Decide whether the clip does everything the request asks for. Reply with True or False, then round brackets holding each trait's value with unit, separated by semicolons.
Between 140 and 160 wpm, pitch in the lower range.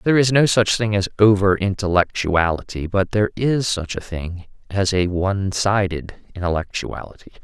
True (155 wpm; 100 Hz)